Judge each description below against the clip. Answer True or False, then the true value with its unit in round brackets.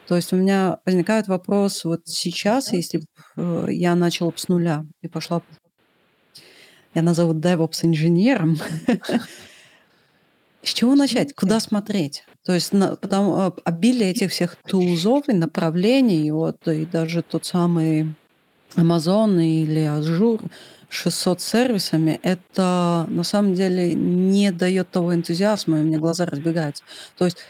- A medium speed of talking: True (130 wpm)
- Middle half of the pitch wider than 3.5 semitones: False (2.9 semitones)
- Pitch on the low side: False (175 Hz)